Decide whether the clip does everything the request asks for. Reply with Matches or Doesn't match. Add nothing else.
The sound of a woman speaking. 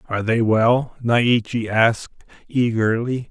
Doesn't match